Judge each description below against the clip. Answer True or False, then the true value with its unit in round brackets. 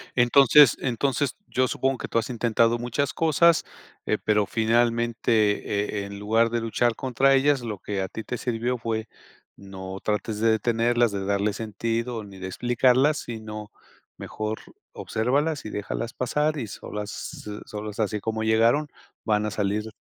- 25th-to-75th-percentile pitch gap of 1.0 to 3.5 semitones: True (2.7 semitones)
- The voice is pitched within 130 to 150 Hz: False (115 Hz)